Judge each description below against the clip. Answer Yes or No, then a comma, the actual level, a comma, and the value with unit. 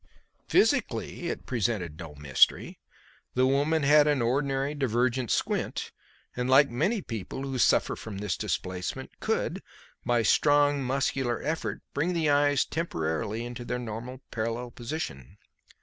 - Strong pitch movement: No, average, 4.2 semitones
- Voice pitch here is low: Yes, low, 125 Hz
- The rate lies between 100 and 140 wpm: Yes, slow, 135 wpm